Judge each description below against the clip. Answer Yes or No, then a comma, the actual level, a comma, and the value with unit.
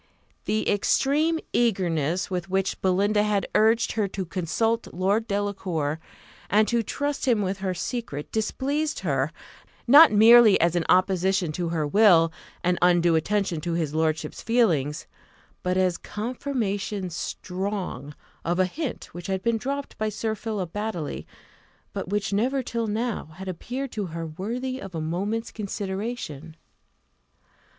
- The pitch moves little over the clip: No, average, 4.5 semitones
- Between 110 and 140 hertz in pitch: No, high, 195 Hz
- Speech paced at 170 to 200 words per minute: No, average, 145 wpm